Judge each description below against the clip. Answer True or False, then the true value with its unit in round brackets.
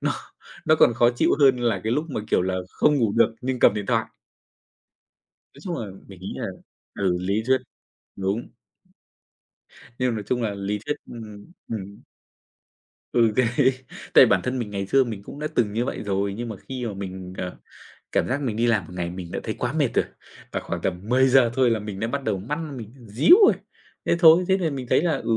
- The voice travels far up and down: False (4.6 semitones)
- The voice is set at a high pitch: False (115 Hz)